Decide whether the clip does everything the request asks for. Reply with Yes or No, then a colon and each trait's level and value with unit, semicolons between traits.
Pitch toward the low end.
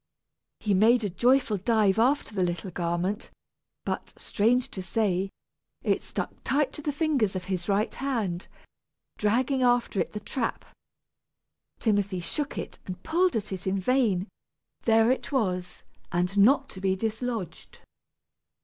No: high, 210 Hz